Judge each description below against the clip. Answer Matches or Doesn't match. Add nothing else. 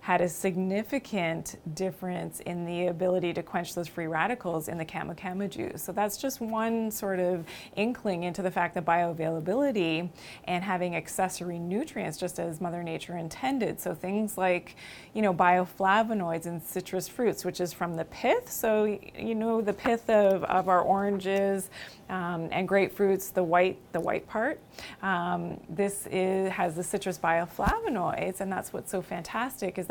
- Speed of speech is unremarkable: Matches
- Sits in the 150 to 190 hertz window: Matches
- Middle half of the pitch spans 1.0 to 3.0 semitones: Matches